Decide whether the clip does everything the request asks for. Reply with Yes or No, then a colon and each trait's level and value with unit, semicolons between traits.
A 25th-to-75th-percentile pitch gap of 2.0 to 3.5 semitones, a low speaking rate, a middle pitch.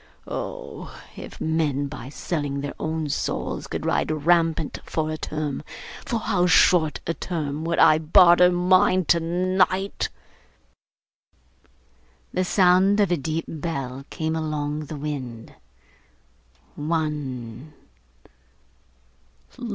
Yes: average, 3.2 semitones; slow, 105 wpm; medium, 160 Hz